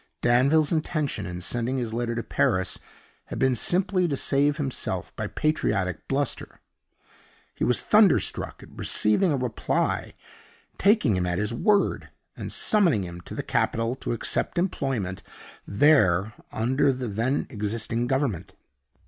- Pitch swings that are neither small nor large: No, wide, 5.7 semitones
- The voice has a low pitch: Yes, low, 125 Hz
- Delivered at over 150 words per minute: No, average, 140 wpm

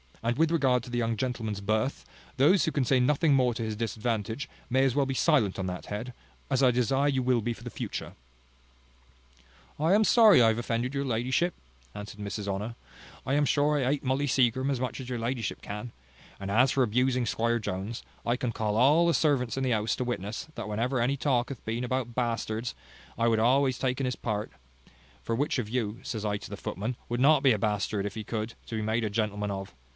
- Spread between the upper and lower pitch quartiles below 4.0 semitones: Yes, average, 3.4 semitones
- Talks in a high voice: No, low, 120 Hz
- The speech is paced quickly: Yes, fast, 225 wpm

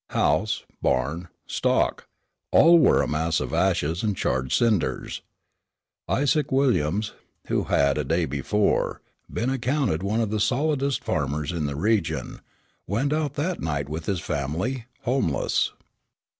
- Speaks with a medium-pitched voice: No, low, 100 Hz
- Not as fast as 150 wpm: Yes, slow, 135 wpm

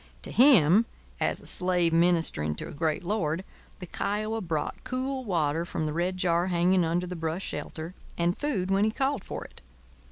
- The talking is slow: No, average, 185 wpm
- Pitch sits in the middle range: Yes, medium, 180 Hz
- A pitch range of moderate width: Yes, average, 3.7 semitones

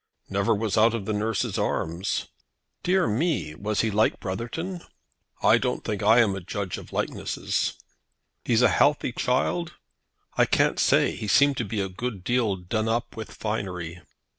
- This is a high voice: No, low, 110 Hz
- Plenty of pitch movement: No, average, 3.8 semitones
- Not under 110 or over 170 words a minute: Yes, average, 165 wpm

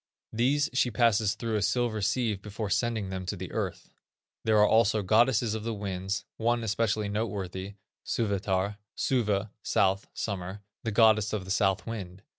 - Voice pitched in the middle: No, low, 105 Hz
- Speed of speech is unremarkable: Yes, average, 160 wpm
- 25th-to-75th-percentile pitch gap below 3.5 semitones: Yes, narrow, 2.6 semitones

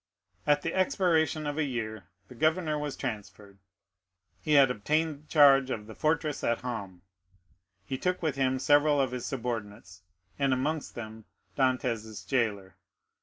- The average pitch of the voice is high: No, low, 130 Hz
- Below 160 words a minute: Yes, average, 145 wpm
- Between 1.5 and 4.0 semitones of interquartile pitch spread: No, average, 5.3 semitones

